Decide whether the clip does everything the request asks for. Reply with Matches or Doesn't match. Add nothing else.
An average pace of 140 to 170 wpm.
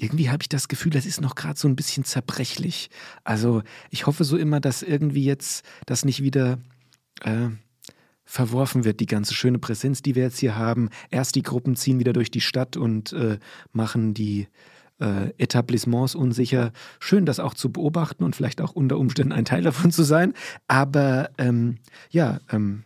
Doesn't match